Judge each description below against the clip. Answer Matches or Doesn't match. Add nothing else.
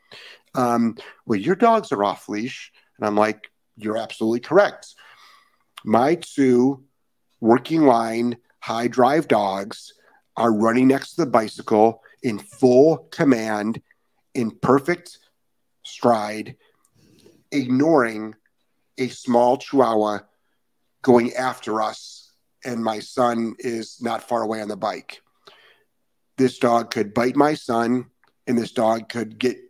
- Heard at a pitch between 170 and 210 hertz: Doesn't match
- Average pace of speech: Doesn't match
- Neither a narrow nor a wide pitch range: Matches